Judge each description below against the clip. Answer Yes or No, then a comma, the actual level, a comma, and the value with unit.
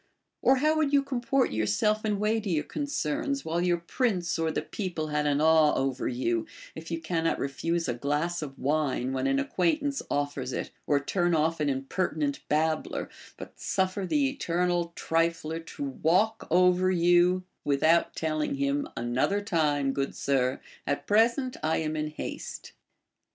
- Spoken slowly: No, average, 155 wpm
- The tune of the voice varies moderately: Yes, average, 4.5 semitones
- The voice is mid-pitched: Yes, medium, 165 Hz